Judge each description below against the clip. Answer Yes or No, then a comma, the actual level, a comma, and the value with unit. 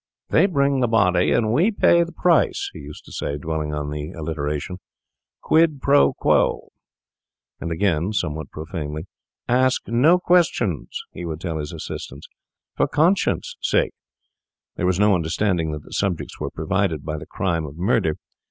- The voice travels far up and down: Yes, wide, 8.1 semitones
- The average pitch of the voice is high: No, very low, 90 Hz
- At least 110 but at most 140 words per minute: No, average, 160 wpm